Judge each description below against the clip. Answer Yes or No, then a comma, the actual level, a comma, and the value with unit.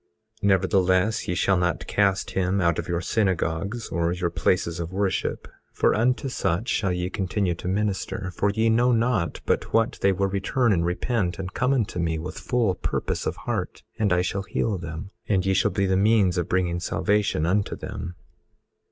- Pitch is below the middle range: Yes, very low, 95 Hz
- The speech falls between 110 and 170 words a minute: No, average, 190 wpm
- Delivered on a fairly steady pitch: No, average, 3.0 semitones